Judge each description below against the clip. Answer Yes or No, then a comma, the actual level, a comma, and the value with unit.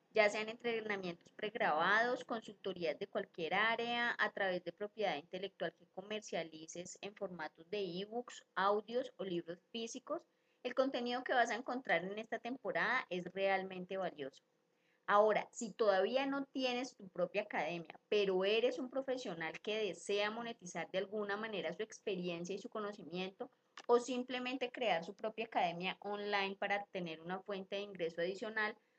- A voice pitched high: Yes, high, 205 Hz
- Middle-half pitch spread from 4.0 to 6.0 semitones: Yes, average, 4.3 semitones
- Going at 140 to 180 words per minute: Yes, average, 150 wpm